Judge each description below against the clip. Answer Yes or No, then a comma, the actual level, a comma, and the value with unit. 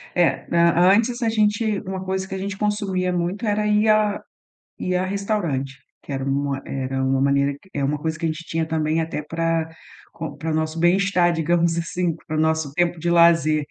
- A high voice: No, medium, 170 Hz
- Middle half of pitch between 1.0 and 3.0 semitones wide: No, average, 3.6 semitones